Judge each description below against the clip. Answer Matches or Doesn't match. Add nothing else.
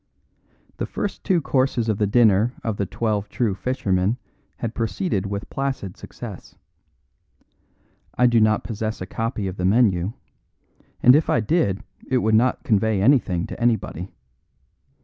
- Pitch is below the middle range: Matches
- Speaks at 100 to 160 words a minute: Matches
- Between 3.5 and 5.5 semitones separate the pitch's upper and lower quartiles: Matches